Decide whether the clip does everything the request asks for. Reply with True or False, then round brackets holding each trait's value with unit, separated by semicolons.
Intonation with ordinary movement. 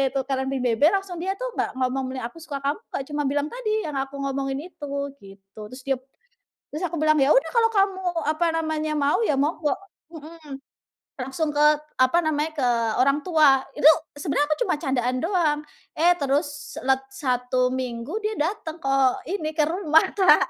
True (3.3 semitones)